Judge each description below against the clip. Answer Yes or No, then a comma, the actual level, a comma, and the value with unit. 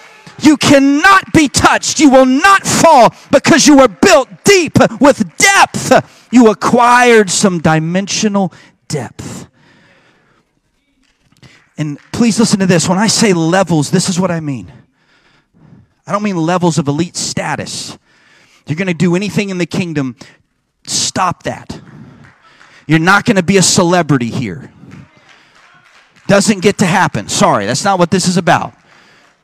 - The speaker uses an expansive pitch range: Yes, wide, 5.8 semitones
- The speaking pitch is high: Yes, high, 195 Hz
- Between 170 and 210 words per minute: No, average, 145 wpm